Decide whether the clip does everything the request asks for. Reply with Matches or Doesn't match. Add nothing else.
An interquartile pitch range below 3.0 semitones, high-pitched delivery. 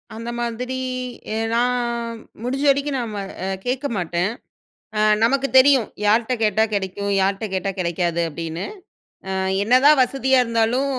Doesn't match